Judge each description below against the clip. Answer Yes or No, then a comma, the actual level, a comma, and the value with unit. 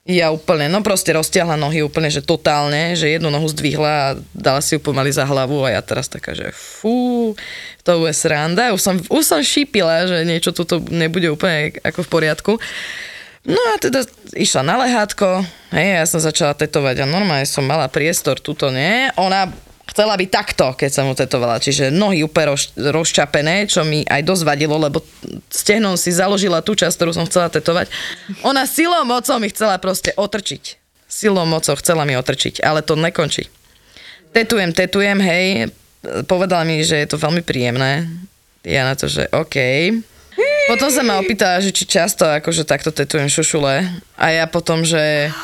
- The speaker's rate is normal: No, fast, 175 wpm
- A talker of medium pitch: Yes, medium, 165 Hz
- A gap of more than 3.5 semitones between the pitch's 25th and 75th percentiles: Yes, average, 4.4 semitones